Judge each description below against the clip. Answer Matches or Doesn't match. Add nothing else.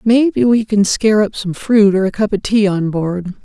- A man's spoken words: Doesn't match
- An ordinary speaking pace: Doesn't match